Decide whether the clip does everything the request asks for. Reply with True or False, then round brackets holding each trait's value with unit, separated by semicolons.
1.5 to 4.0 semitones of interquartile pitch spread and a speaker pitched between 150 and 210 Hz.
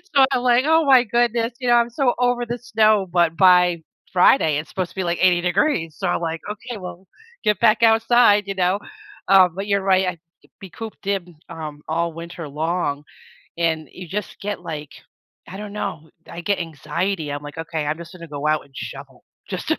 False (4.8 semitones; 185 Hz)